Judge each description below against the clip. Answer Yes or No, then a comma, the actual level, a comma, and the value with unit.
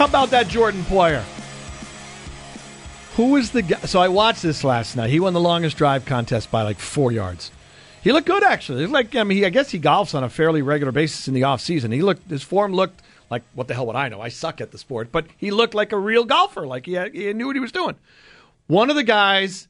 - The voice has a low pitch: No, medium, 170 Hz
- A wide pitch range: Yes, wide, 8.9 semitones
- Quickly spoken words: Yes, fast, 250 wpm